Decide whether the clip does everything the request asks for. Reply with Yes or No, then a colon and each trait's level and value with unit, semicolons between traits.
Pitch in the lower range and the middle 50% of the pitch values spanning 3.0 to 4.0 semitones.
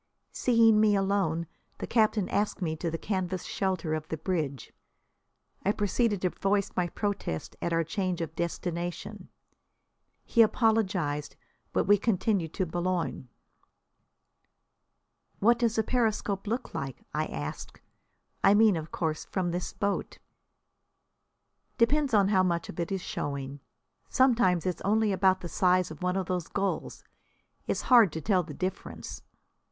No: medium, 185 Hz; average, 3.7 semitones